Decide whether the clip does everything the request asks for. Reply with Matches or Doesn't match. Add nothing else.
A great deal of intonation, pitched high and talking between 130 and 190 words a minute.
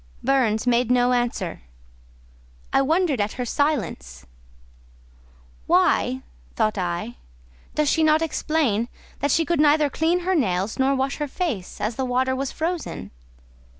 Matches